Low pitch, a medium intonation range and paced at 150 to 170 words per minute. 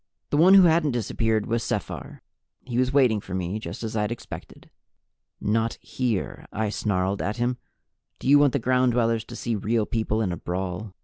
No: low, 115 Hz; average, 3.3 semitones; average, 190 wpm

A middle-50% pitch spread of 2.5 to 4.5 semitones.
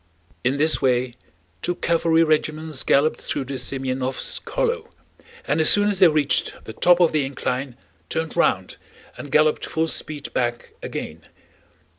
Yes: average, 3.8 semitones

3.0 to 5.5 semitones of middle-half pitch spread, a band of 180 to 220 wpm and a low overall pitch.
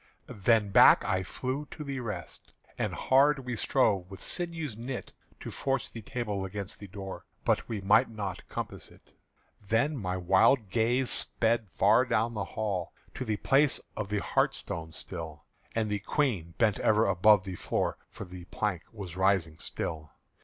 No: average, 4.2 semitones; average, 165 wpm; low, 105 Hz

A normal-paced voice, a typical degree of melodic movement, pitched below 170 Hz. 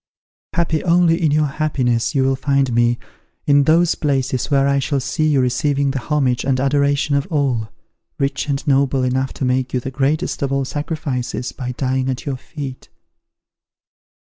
No: average, 170 wpm; narrow, 2.1 semitones; medium, 140 Hz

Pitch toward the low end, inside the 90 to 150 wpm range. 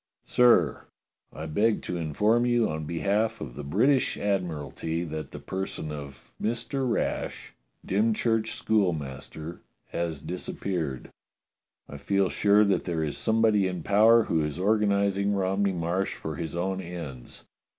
Yes: very low, 95 Hz; average, 140 wpm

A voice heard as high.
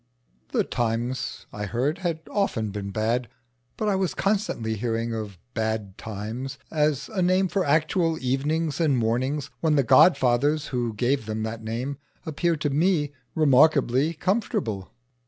No: low, 135 Hz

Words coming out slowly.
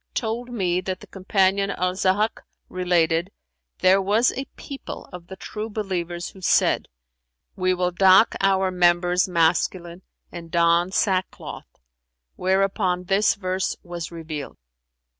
Yes: slow, 125 wpm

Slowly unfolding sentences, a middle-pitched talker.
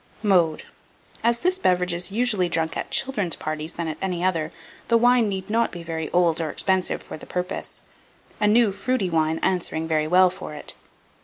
No: average, 190 wpm; medium, 180 Hz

